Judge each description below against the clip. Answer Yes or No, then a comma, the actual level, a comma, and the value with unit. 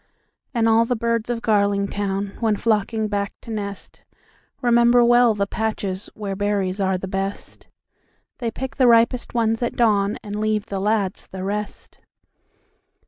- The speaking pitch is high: Yes, high, 215 Hz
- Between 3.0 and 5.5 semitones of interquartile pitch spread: No, narrow, 2.6 semitones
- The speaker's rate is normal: No, slow, 130 wpm